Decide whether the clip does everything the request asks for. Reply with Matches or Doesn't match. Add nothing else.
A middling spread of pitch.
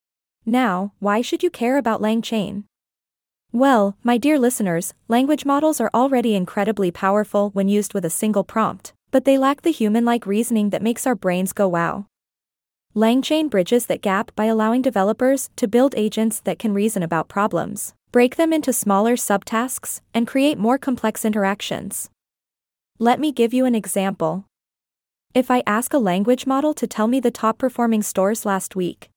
Matches